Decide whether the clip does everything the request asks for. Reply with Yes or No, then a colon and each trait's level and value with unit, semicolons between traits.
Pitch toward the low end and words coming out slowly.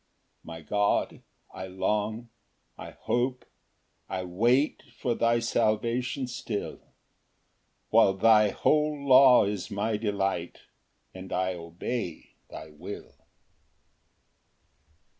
Yes: low, 105 Hz; slow, 100 wpm